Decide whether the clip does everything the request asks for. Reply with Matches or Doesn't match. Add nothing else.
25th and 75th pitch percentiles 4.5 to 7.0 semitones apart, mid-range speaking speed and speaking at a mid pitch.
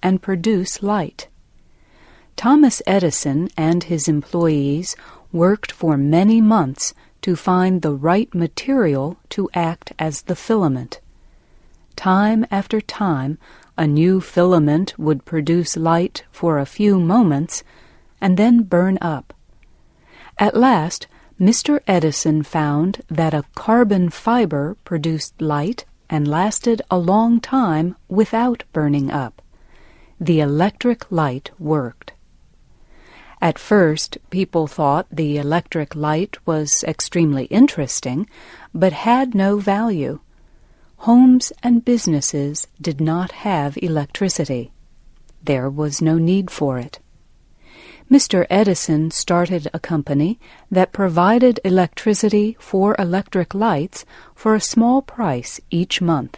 Doesn't match